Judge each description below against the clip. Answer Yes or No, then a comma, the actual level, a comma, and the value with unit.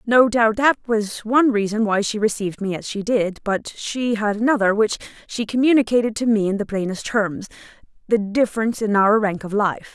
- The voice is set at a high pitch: Yes, high, 215 Hz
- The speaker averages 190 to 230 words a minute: Yes, average, 195 wpm